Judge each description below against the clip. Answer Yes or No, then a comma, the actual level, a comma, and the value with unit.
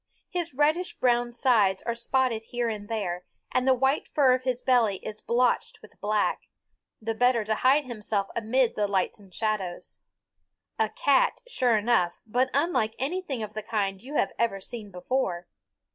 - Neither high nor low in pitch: No, high, 235 Hz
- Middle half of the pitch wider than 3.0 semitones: Yes, average, 3.6 semitones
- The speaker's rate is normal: Yes, average, 170 wpm